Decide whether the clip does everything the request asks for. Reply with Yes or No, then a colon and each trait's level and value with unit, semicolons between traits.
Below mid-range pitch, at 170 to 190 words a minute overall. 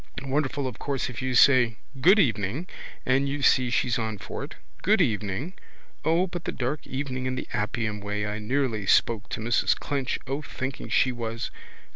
Yes: low, 130 Hz; average, 180 wpm